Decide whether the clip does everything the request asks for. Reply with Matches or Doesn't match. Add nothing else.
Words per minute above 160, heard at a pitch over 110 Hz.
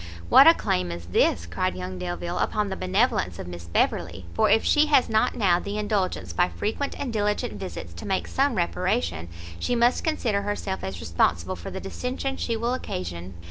Matches